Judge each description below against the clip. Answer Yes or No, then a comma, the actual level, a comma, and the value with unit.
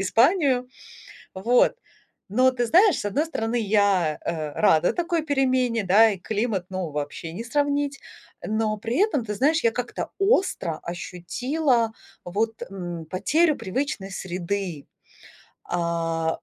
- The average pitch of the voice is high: Yes, high, 220 Hz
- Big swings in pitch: Yes, wide, 6.9 semitones